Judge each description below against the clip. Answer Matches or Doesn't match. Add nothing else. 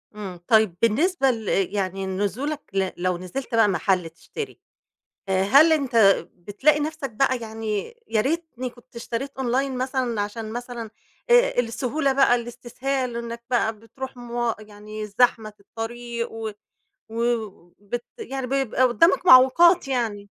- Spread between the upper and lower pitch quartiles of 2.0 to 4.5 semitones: Matches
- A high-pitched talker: Matches